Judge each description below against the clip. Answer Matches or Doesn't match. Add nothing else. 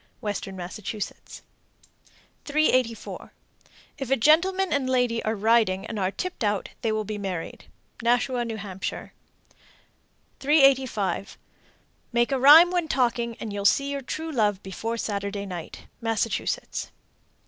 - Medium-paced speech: Doesn't match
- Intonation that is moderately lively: Matches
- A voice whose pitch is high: Matches